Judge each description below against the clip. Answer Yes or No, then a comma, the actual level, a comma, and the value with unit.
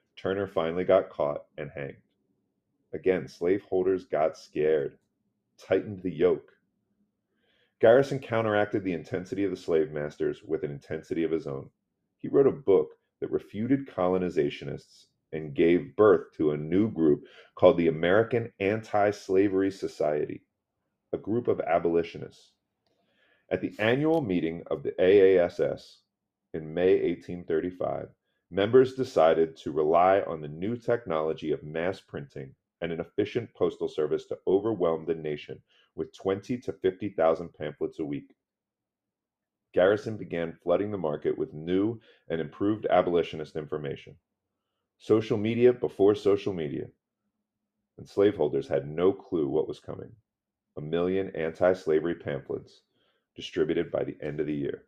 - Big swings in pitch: Yes, wide, 9.0 semitones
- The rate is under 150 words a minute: Yes, slow, 135 wpm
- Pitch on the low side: Yes, very low, 95 Hz